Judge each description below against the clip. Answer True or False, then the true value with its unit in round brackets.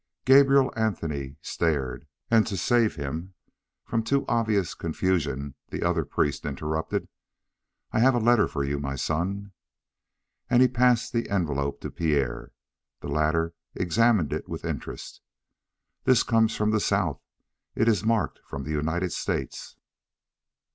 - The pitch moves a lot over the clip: True (7.3 semitones)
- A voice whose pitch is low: True (90 Hz)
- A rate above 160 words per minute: False (140 wpm)